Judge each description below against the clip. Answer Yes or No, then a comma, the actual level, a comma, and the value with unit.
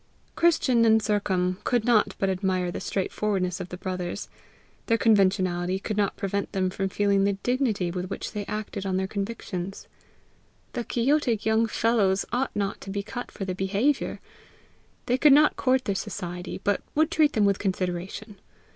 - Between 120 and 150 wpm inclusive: No, average, 170 wpm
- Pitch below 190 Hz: No, high, 200 Hz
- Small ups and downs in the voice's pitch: No, average, 3.4 semitones